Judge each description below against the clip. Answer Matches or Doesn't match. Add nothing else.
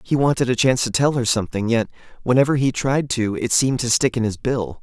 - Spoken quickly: Matches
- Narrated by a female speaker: Doesn't match